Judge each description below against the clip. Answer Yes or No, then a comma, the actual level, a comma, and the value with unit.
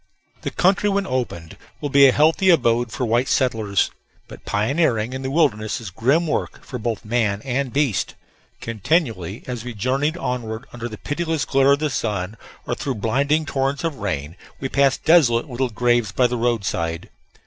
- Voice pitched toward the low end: Yes, low, 125 Hz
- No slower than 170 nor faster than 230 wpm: Yes, average, 175 wpm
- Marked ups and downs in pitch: No, average, 4.2 semitones